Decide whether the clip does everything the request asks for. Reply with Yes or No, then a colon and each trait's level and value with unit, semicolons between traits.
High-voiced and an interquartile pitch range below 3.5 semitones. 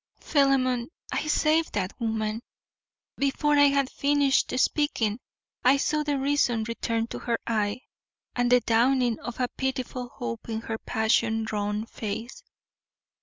No: high, 245 Hz; average, 3.8 semitones